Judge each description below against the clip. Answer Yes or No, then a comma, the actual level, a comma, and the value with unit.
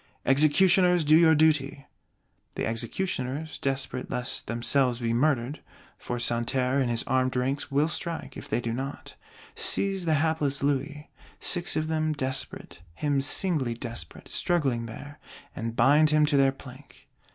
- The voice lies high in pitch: No, medium, 140 Hz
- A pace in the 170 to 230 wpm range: No, average, 145 wpm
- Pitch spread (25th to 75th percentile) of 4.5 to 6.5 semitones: No, average, 3.6 semitones